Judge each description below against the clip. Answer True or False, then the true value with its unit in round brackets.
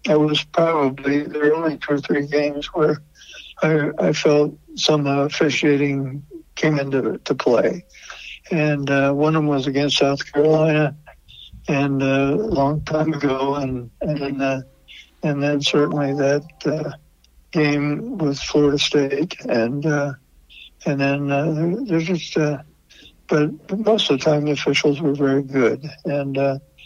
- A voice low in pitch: False (145 Hz)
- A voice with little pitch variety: True (1.6 semitones)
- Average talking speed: True (150 wpm)